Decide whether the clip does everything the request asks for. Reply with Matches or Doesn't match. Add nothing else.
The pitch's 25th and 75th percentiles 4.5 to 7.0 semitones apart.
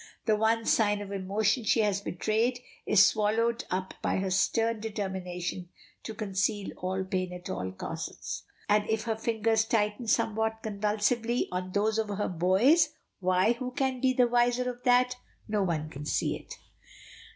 Doesn't match